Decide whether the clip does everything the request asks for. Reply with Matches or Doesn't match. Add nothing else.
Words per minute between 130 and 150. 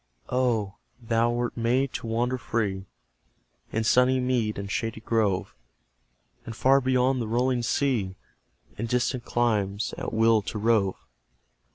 Matches